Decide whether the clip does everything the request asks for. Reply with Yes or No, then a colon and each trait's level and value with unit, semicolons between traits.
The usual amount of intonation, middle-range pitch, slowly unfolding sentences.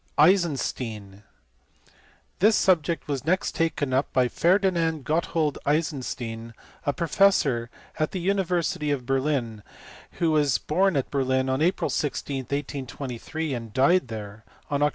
Yes: average, 4.4 semitones; medium, 145 Hz; slow, 130 wpm